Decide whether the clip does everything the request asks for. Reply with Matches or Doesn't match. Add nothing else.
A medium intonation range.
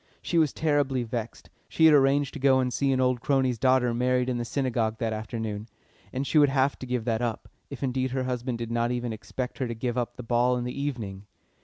Doesn't match